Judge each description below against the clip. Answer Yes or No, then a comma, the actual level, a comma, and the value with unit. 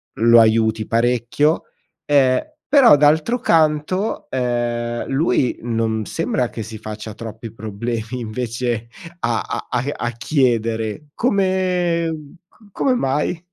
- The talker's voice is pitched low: Yes, low, 120 Hz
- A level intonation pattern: No, average, 5.2 semitones